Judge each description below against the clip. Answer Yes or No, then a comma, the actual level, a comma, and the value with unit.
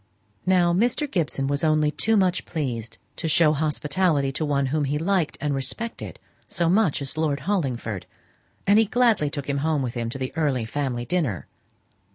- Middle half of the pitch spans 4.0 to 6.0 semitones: Yes, average, 4.7 semitones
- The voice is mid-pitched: Yes, medium, 150 Hz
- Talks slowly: No, average, 180 wpm